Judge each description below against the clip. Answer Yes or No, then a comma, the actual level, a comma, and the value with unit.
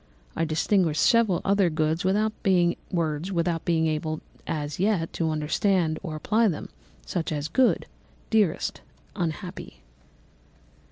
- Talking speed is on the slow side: Yes, slow, 110 wpm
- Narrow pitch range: No, average, 3.7 semitones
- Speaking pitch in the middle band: Yes, medium, 170 Hz